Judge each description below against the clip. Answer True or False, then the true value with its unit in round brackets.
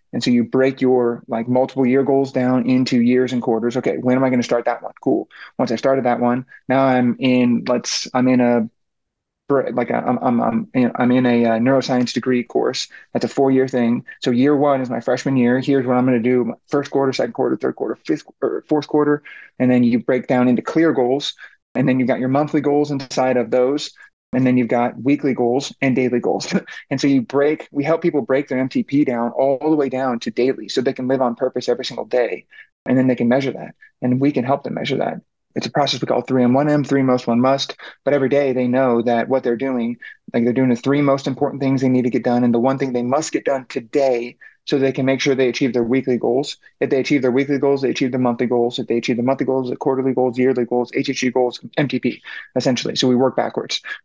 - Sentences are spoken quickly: True (245 wpm)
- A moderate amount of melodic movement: False (1.8 semitones)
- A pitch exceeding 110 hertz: True (130 Hz)